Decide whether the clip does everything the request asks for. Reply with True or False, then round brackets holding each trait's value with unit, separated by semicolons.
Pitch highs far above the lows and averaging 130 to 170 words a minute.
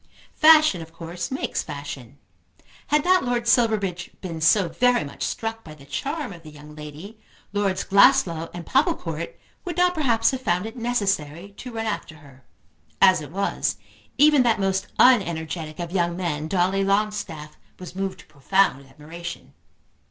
True (6.0 semitones; 160 wpm)